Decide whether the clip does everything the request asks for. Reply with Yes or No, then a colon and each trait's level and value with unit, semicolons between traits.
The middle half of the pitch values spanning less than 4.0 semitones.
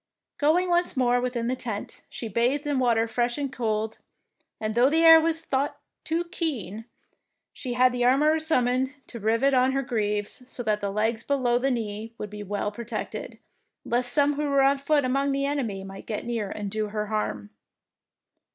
No: average, 4.3 semitones